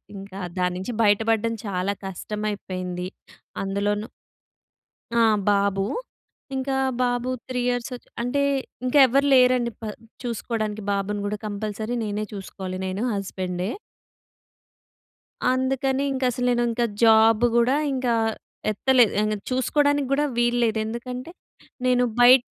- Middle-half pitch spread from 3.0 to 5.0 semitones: Yes, average, 3.7 semitones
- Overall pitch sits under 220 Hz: No, high, 225 Hz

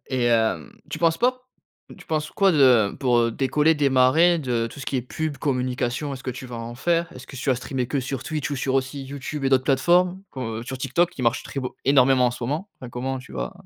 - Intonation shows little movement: No, average, 3.2 semitones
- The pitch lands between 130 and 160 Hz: Yes, low, 135 Hz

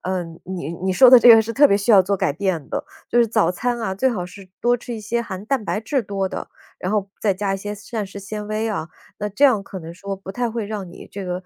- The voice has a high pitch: Yes, high, 200 Hz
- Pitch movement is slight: No, average, 3.2 semitones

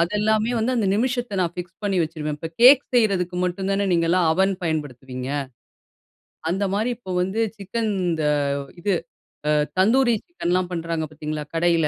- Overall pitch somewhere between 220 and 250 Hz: No, medium, 185 Hz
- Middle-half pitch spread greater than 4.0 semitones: Yes, average, 4.7 semitones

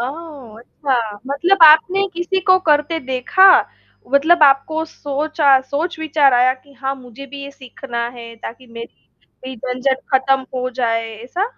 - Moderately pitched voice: No, very high, 275 Hz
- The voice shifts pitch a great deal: No, average, 3.7 semitones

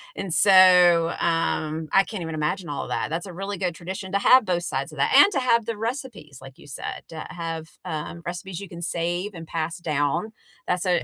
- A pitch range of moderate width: Yes, average, 3.0 semitones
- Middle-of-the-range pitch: Yes, medium, 175 Hz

